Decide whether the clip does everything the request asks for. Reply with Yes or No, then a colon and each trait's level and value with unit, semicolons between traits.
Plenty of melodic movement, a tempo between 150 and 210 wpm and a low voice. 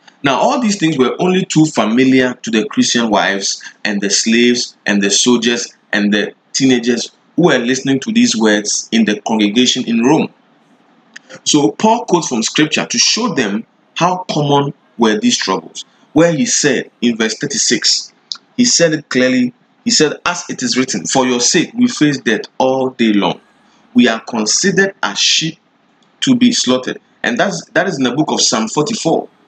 Yes: wide, 7.9 semitones; average, 180 wpm; low, 130 Hz